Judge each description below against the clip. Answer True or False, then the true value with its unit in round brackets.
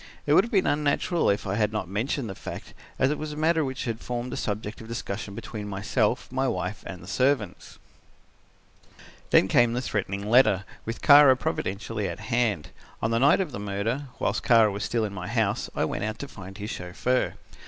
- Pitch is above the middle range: False (110 Hz)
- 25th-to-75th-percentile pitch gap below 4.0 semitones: False (4.3 semitones)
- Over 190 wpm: True (205 wpm)